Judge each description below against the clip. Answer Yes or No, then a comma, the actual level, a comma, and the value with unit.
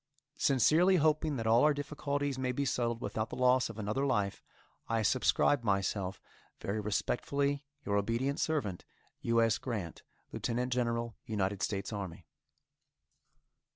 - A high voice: No, low, 120 Hz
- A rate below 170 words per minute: Yes, slow, 135 wpm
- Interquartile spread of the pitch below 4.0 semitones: No, average, 5.2 semitones